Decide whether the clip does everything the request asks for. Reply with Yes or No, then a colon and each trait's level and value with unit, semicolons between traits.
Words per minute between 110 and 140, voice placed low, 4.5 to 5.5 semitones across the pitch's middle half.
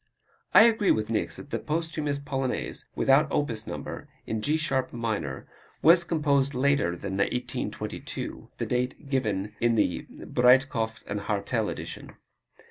Yes: slow, 135 wpm; low, 130 Hz; average, 4.9 semitones